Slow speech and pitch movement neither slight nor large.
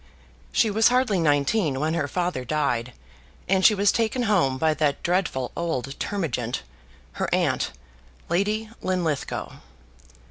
No: slow, 130 wpm; wide, 6.3 semitones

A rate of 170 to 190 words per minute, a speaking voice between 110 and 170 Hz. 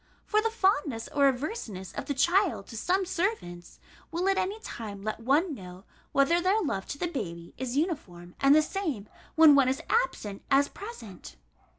No: average, 180 wpm; very high, 280 Hz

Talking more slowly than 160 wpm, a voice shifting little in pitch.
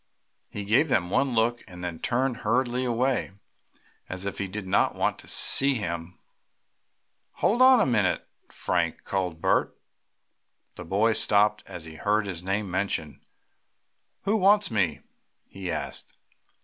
No: average, 150 wpm; average, 5.2 semitones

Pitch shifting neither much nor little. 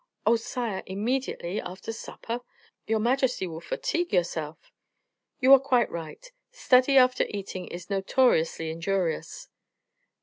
No: wide, 6.5 semitones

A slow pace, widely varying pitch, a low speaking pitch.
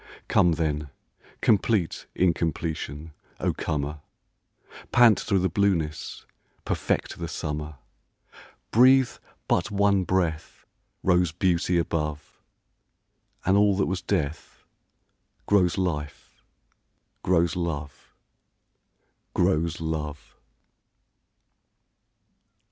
No: slow, 80 wpm; average, 3.8 semitones; very low, 85 Hz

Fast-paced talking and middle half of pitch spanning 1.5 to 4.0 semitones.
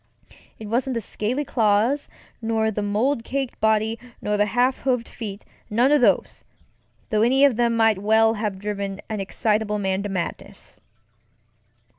No: average, 155 wpm; narrow, 2.6 semitones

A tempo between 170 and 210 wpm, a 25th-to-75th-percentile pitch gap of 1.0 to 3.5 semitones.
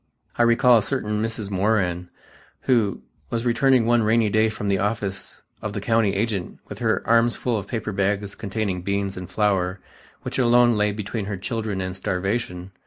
Yes: average, 175 wpm; average, 2.9 semitones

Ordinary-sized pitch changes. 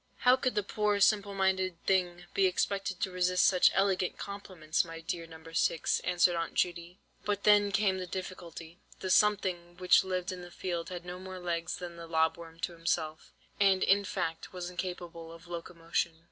No: narrow, 2.2 semitones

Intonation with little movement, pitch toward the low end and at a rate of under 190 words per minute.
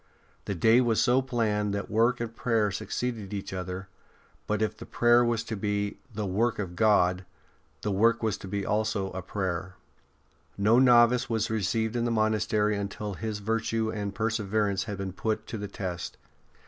Yes: narrow, 2.3 semitones; low, 105 Hz; average, 180 wpm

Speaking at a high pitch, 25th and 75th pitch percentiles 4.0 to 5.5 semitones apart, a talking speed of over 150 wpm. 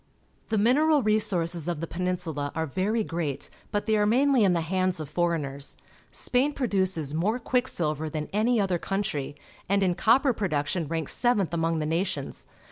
No: medium, 180 Hz; average, 5.1 semitones; average, 170 wpm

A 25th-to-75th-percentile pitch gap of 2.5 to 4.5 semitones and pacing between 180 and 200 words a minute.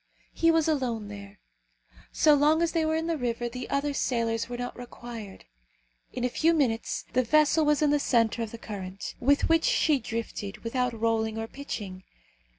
No: average, 4.9 semitones; average, 185 wpm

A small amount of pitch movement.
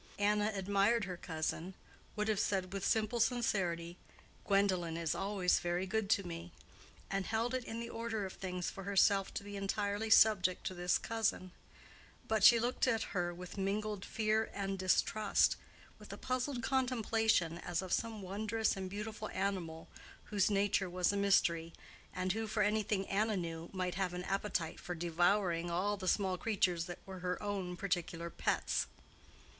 No: average, 3.1 semitones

